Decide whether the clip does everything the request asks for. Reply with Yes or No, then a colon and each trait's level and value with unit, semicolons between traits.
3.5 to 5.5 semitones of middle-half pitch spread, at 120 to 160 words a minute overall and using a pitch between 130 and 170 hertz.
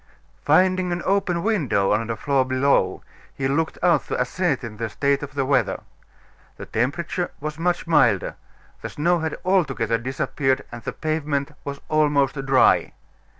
Yes: average, 4.5 semitones; average, 150 wpm; medium, 140 Hz